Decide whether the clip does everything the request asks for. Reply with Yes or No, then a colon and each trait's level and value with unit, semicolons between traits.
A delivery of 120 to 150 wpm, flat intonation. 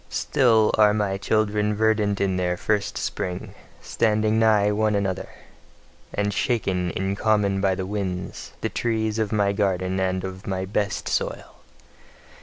Yes: average, 145 wpm; narrow, 2.2 semitones